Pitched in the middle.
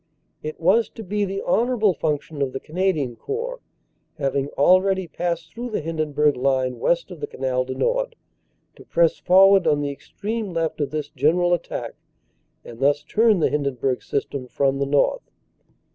Yes: medium, 160 Hz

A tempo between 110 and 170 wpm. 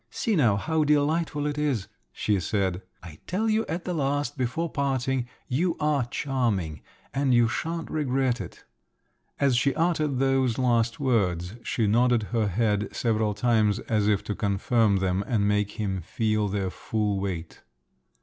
Yes: average, 160 wpm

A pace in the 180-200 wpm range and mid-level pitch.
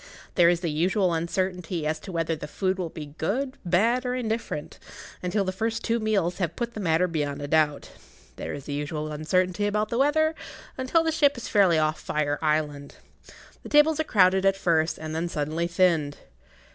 Yes: average, 195 wpm; medium, 180 Hz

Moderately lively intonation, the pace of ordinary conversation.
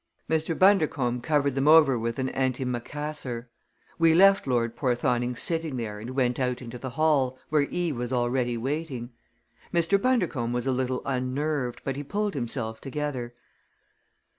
Yes: average, 4.0 semitones; average, 150 wpm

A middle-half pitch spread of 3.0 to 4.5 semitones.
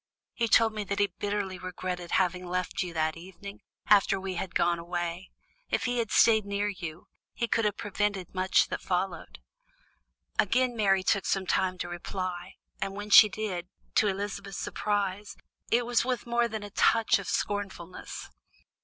No: narrow, 2.4 semitones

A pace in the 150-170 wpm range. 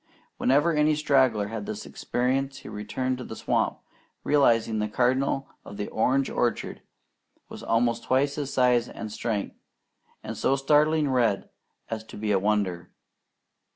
Yes: average, 155 wpm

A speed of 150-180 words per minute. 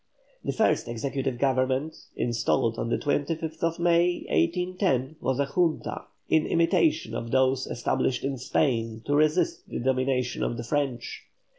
No: average, 140 wpm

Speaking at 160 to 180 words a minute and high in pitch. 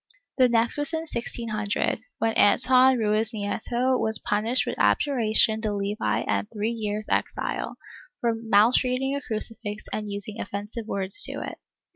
No: average, 145 wpm; high, 220 Hz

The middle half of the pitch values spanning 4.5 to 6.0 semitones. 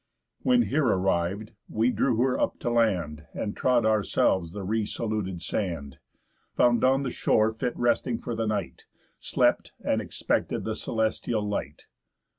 No: average, 4.0 semitones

